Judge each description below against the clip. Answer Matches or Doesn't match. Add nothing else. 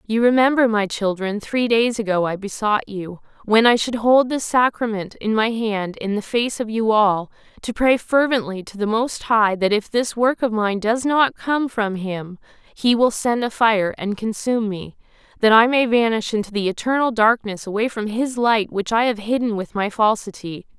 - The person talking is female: Matches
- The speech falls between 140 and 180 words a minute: Doesn't match